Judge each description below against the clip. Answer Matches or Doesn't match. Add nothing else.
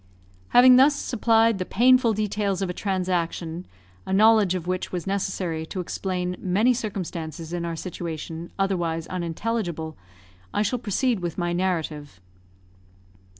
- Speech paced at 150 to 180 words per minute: Doesn't match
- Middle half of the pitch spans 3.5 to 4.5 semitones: Matches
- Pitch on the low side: Doesn't match